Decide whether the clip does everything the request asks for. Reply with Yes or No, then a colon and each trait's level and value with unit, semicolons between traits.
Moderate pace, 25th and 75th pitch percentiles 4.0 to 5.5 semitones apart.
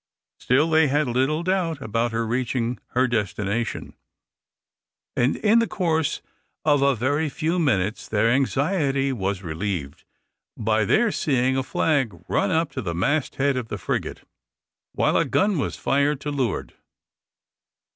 Yes: average, 145 wpm; average, 5.2 semitones